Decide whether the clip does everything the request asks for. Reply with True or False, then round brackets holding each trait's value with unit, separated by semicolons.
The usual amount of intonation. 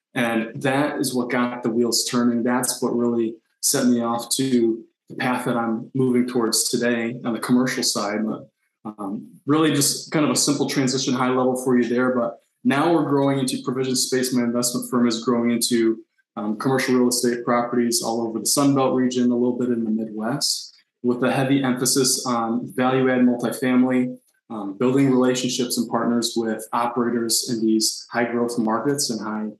False (1.6 semitones)